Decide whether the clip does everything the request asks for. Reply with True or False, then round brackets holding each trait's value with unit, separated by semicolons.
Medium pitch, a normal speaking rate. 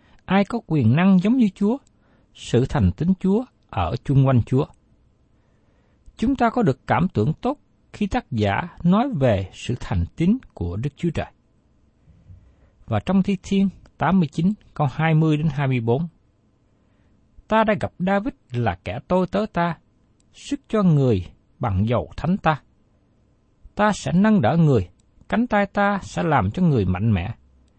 False (150 Hz; 160 wpm)